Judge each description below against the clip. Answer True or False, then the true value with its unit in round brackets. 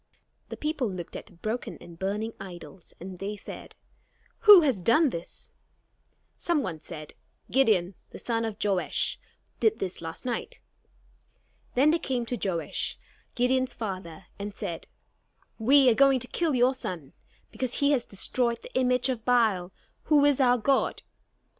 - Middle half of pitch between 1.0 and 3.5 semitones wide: False (5.6 semitones)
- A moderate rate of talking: True (155 wpm)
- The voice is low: False (230 Hz)